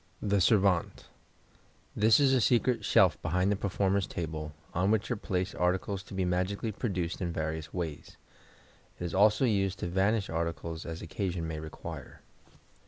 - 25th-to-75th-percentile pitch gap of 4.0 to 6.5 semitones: No, average, 3.4 semitones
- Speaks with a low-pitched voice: Yes, very low, 95 Hz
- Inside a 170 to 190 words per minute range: No, average, 155 wpm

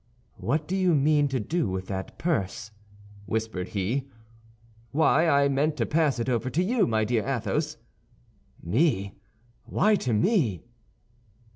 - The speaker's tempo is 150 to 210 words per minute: No, average, 140 wpm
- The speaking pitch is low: Yes, low, 130 Hz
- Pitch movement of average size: No, wide, 6.4 semitones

